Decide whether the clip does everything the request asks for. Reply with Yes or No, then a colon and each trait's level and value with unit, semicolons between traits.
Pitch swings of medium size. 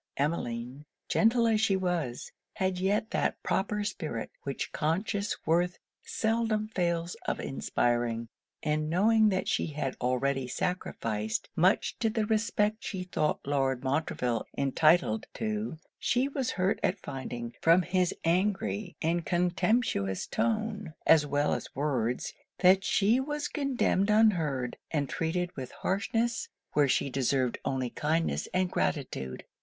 No: wide, 7.3 semitones